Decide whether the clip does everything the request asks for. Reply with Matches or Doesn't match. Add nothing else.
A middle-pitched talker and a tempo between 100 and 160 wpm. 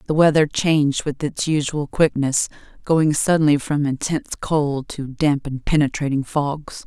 Matches